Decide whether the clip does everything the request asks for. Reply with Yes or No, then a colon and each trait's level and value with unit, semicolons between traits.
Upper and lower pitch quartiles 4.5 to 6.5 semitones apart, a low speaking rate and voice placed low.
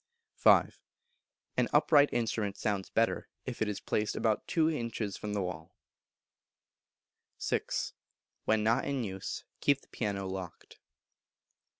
No: average, 3.7 semitones; slow, 115 wpm; low, 110 Hz